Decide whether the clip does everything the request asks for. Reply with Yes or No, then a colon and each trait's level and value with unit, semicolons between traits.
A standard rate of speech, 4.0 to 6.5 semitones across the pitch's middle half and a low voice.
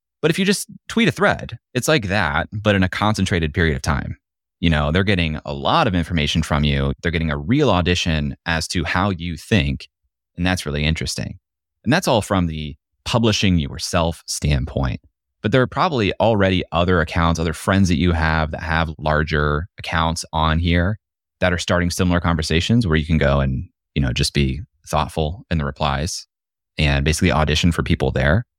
No: average, 190 wpm; average, 3.4 semitones; very low, 85 Hz